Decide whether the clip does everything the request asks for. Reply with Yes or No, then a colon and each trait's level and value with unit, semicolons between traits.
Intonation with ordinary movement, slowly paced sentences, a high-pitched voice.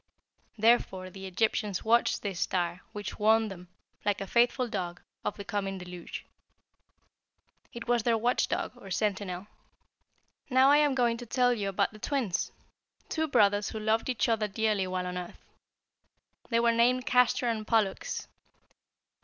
No: average, 3.6 semitones; average, 155 wpm; high, 215 Hz